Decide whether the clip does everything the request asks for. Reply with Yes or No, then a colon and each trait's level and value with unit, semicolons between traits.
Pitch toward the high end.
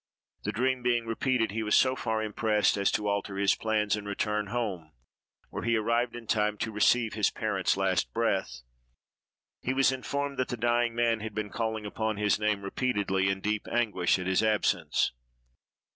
No: low, 110 Hz